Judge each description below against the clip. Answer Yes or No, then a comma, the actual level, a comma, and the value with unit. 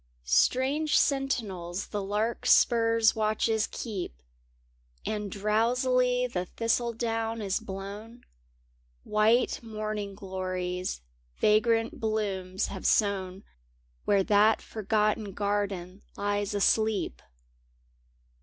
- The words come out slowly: Yes, slow, 80 wpm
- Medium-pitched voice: No, high, 215 Hz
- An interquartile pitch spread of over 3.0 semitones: No, average, 2.7 semitones